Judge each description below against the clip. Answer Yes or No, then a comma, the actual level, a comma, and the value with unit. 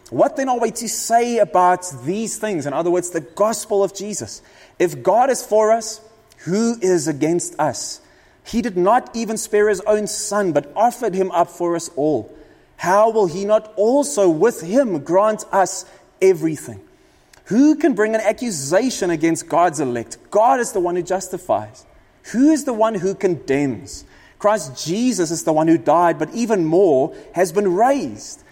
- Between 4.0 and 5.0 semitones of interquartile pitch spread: Yes, average, 4.7 semitones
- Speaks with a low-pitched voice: No, high, 205 Hz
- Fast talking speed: No, average, 175 wpm